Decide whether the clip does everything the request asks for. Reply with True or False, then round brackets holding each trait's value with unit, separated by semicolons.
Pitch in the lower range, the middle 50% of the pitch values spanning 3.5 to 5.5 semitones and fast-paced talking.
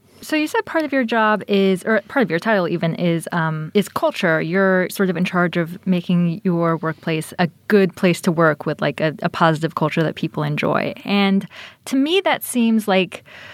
False (185 Hz; 4.4 semitones; 210 wpm)